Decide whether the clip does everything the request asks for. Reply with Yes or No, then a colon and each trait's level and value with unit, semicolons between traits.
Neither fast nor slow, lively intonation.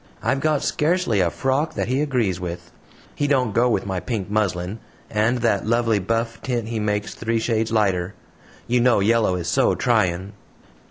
No: average, 175 wpm; average, 3.8 semitones